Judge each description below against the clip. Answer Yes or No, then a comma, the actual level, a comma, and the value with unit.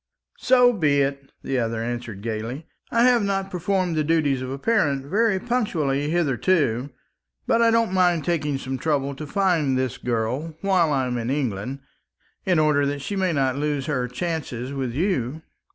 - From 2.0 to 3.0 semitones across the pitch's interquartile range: No, wide, 5.6 semitones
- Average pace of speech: Yes, average, 175 wpm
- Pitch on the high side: No, medium, 145 Hz